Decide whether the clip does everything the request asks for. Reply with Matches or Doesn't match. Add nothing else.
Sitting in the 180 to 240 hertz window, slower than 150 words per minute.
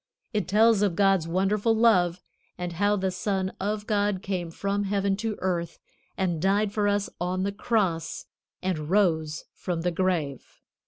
Doesn't match